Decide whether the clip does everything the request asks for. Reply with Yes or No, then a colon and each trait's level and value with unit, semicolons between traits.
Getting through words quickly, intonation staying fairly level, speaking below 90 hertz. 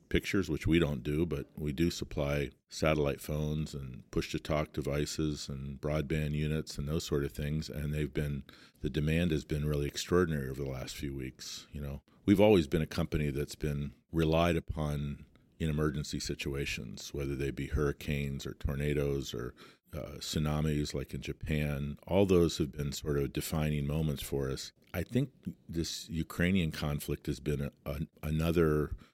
No: average, 175 wpm; narrow, 1.8 semitones; very low, 75 Hz